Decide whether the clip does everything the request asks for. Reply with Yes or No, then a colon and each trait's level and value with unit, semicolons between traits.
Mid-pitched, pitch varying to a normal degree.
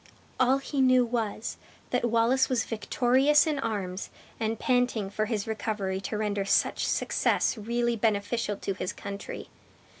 No: high, 225 Hz; average, 3.4 semitones